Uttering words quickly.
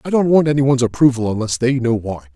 Yes: fast, 230 wpm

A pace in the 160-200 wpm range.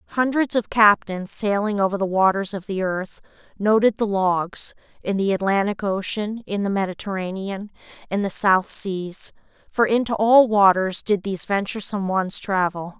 No: average, 150 wpm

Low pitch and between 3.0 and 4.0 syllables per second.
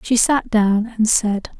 No: high, 220 Hz; 3.6 syllables/s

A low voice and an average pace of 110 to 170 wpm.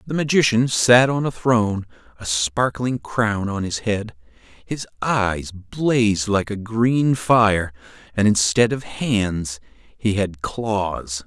Yes: low, 105 Hz; average, 140 wpm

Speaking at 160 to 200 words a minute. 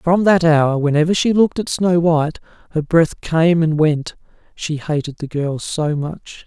Yes: average, 185 wpm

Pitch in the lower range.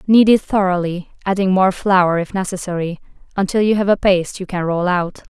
No: medium, 185 Hz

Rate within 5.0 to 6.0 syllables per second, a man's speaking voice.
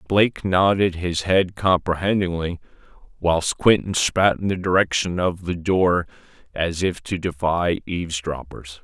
No: 4.3 syllables/s; male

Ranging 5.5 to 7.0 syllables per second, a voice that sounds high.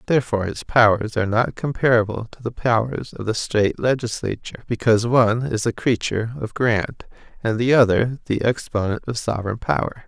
No: 5.9 syllables/s; low, 115 Hz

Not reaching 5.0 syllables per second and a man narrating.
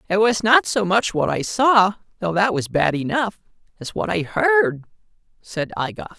Yes: 4.4 syllables/s; male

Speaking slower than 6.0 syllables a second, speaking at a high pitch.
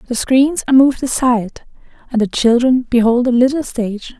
Yes: 5.7 syllables/s; high, 245 Hz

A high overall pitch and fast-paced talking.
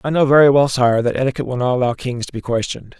No: low, 130 Hz; fast, 280 wpm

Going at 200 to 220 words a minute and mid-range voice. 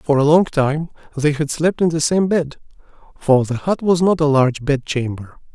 Yes: fast, 205 wpm; medium, 150 Hz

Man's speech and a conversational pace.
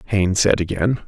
Yes: male; average, 165 wpm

